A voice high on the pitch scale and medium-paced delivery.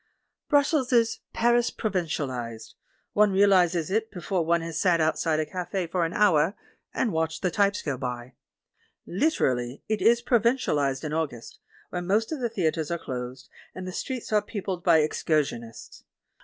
No: medium, 175 Hz; average, 165 wpm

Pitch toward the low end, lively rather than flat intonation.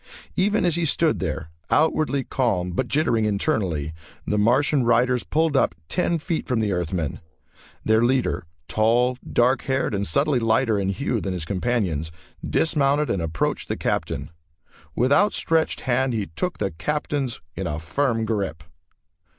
Yes: low, 120 Hz; wide, 6.5 semitones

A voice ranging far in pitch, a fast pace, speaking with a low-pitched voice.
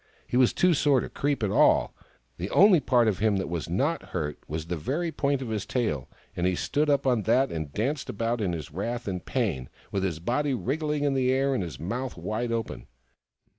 Yes: wide, 7.0 semitones; fast, 220 wpm; low, 115 Hz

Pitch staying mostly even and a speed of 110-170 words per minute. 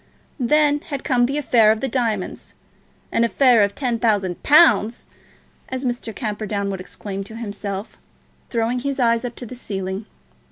No: average, 3.7 semitones; average, 160 wpm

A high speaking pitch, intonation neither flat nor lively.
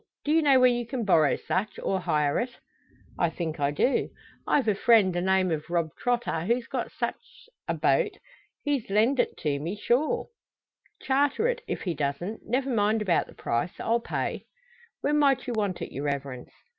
No: high, 210 Hz; wide, 7.1 semitones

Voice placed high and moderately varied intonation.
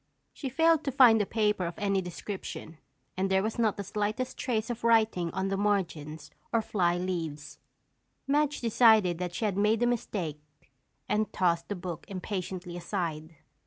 Yes: high, 195 Hz; average, 4.1 semitones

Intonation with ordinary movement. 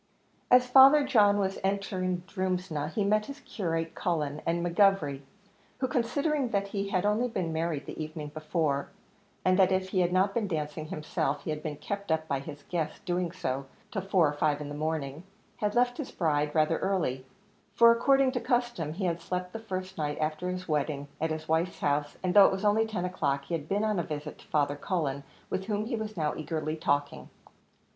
Yes: average, 4.9 semitones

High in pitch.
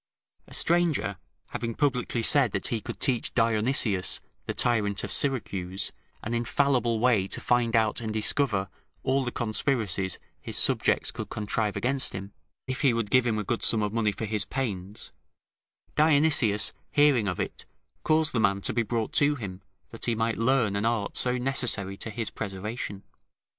No: low, 115 Hz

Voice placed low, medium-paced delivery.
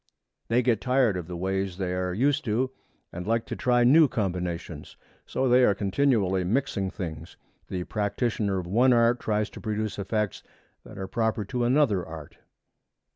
Yes: low, 105 Hz; average, 170 wpm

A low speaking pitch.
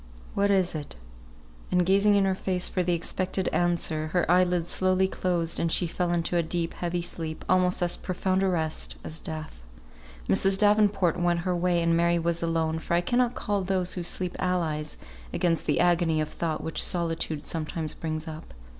No: medium, 175 Hz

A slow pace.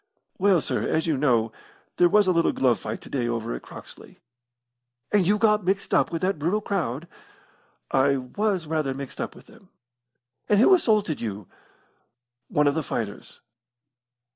No: average, 165 wpm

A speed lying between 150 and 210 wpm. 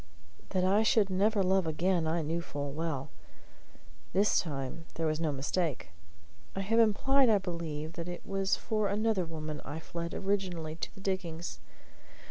Yes: average, 160 wpm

